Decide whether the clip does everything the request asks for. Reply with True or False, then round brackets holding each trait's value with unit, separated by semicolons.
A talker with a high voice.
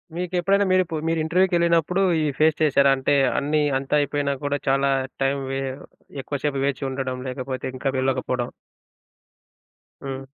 False (145 Hz)